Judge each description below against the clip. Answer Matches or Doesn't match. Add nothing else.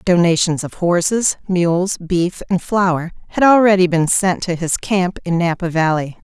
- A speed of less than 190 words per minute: Matches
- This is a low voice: Doesn't match